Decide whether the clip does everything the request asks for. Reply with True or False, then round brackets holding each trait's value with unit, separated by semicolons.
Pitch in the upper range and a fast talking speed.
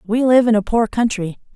True (225 Hz; 230 wpm)